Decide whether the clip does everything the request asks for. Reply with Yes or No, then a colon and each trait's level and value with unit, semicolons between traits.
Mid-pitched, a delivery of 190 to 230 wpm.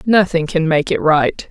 Yes: medium, 170 Hz; average, 200 wpm